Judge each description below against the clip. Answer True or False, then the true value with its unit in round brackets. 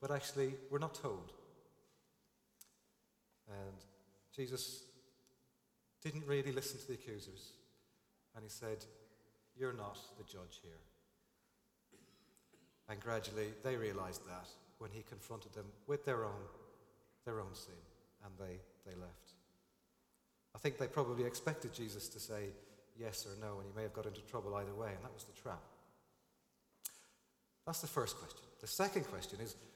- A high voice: False (110 Hz)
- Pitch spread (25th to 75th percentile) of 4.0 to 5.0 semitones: True (4.4 semitones)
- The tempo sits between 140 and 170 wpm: True (145 wpm)